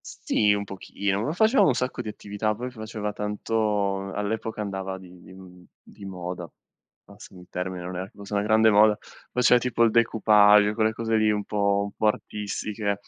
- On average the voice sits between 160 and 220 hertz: No, low, 105 Hz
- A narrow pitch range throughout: Yes, narrow, 2.0 semitones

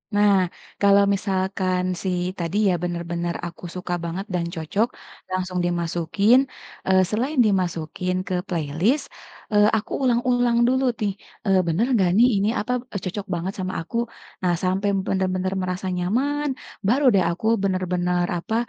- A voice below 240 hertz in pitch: Yes, medium, 185 Hz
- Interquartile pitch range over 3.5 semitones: No, average, 2.8 semitones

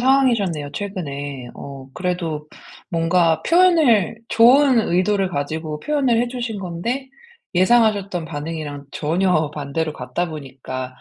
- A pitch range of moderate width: No, wide, 7.1 semitones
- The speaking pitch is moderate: Yes, medium, 175 Hz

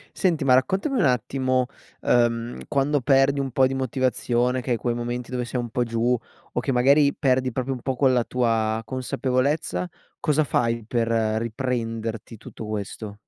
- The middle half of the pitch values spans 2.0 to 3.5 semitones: Yes, narrow, 2.4 semitones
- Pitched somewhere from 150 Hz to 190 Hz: No, low, 125 Hz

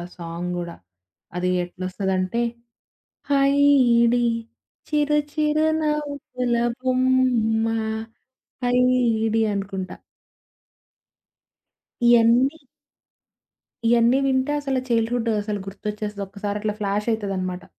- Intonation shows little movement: No, average, 4.3 semitones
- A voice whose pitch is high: Yes, high, 230 Hz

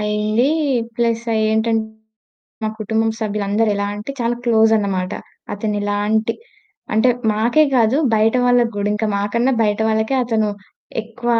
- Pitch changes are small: Yes, narrow, 1.5 semitones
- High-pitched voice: Yes, high, 220 Hz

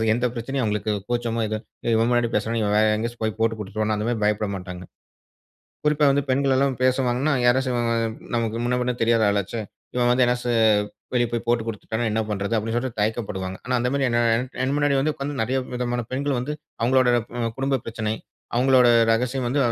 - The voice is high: No, low, 120 Hz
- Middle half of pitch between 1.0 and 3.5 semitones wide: Yes, average, 2.7 semitones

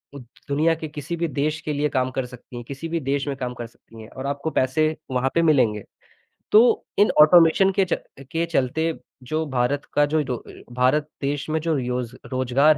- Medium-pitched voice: Yes, medium, 145 Hz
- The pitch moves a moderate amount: Yes, average, 3.8 semitones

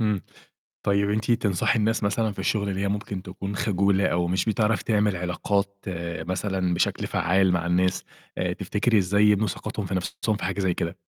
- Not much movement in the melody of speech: Yes, narrow, 2.3 semitones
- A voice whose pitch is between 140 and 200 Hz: No, low, 100 Hz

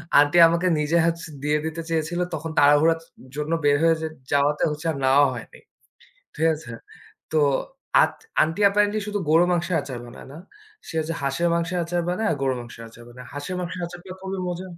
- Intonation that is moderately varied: Yes, average, 3.3 semitones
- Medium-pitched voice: Yes, medium, 160 Hz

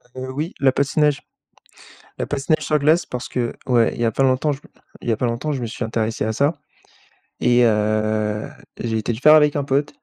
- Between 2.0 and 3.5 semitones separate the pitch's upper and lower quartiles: No, average, 4.2 semitones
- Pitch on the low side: Yes, low, 130 Hz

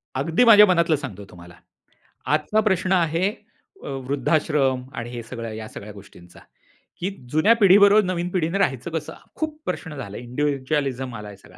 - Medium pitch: Yes, medium, 150 Hz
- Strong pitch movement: Yes, wide, 7.0 semitones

